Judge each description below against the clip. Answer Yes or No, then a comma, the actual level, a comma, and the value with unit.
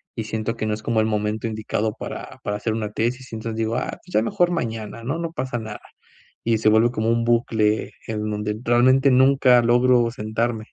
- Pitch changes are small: Yes, narrow, 2.0 semitones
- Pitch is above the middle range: No, low, 115 Hz